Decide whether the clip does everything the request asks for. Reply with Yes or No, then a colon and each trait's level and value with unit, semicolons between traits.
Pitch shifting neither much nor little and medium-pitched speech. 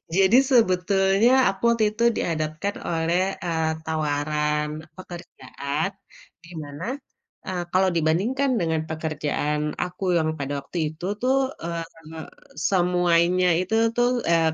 Yes: average, 3.1 semitones; medium, 170 Hz